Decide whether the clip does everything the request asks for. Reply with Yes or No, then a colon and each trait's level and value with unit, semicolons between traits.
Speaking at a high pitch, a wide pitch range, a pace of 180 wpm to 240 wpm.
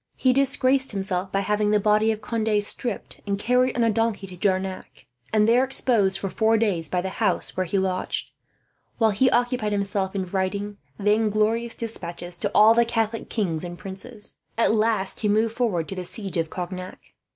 No: high, 210 Hz; average, 3.0 semitones; average, 185 wpm